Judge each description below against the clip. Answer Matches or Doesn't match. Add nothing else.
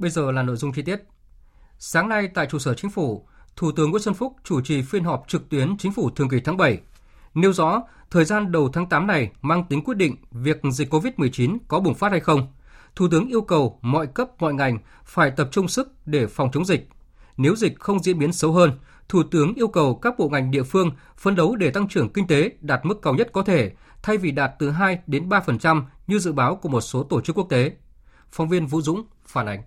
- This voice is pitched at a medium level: Matches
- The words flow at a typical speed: Matches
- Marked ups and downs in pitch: Matches